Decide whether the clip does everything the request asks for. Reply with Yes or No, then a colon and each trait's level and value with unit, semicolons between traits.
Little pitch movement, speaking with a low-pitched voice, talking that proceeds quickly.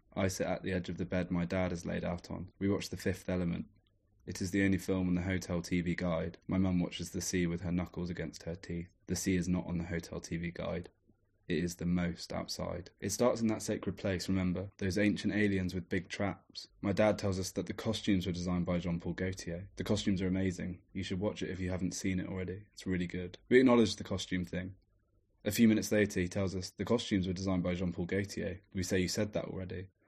Yes: narrow, 1.9 semitones; very low, 95 Hz; fast, 240 wpm